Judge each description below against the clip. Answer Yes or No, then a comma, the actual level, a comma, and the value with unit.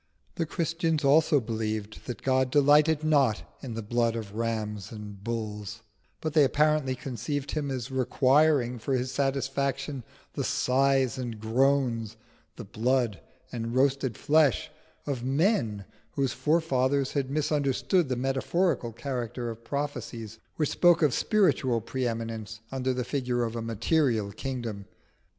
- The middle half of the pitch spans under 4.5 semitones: Yes, average, 3.8 semitones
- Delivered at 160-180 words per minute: No, average, 140 wpm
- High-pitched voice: No, low, 130 Hz